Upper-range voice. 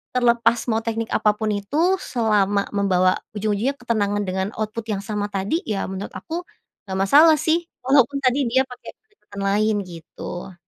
Yes: high, 220 Hz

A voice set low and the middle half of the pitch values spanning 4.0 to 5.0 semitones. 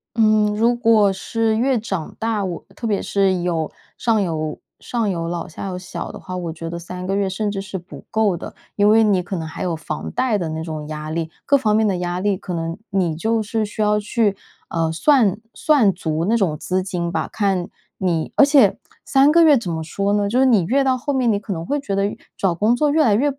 No: high, 200 Hz; average, 4.6 semitones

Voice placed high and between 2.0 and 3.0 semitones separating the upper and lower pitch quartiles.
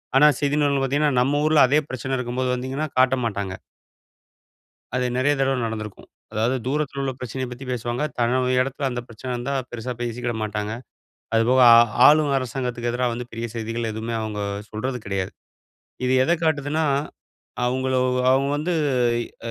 No: low, 125 Hz; narrow, 2.6 semitones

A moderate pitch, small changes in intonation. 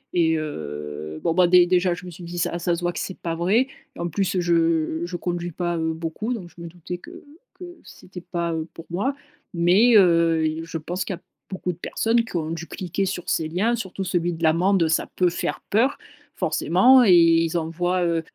Yes: medium, 175 Hz; narrow, 1.9 semitones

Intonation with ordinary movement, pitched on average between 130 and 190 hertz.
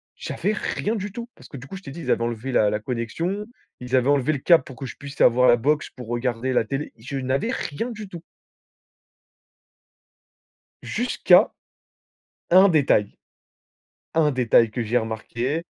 No: wide, 5.8 semitones; low, 135 Hz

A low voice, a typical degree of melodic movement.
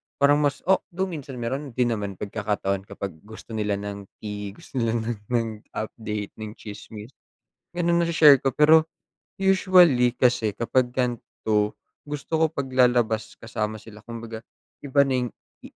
Yes: low, 120 Hz; average, 4.7 semitones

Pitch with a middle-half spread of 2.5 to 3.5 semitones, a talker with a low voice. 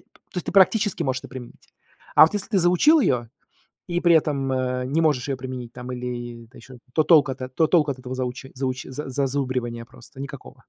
No: average, 4.0 semitones; low, 130 Hz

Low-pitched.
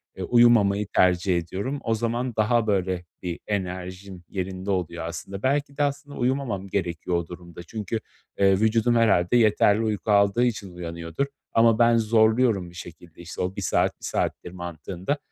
Yes: low, 100 Hz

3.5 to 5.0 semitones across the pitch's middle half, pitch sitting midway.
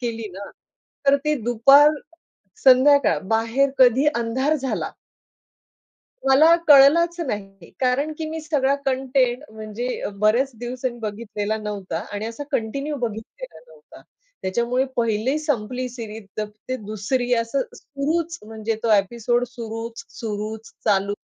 No: average, 4.0 semitones; high, 240 Hz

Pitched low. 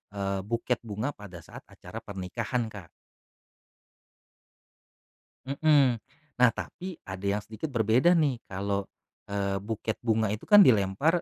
Yes: low, 110 Hz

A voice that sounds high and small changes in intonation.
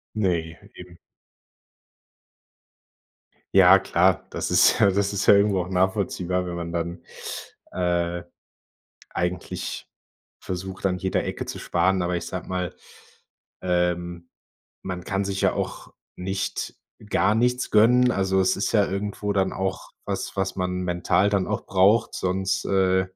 No: very low, 95 Hz; narrow, 1.7 semitones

